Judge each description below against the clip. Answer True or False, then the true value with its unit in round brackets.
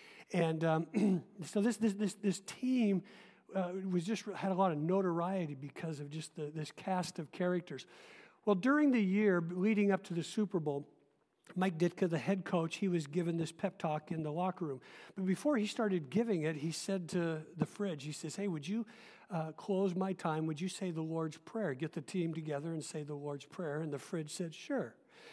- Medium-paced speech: False (210 wpm)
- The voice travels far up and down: False (3.8 semitones)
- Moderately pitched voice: True (180 Hz)